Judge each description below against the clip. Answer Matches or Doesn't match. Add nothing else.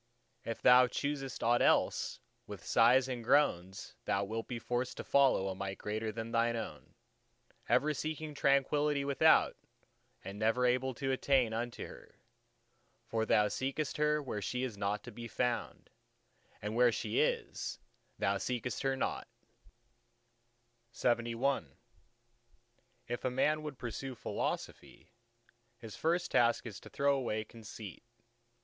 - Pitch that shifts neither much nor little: Matches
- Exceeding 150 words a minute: Doesn't match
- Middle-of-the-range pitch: Doesn't match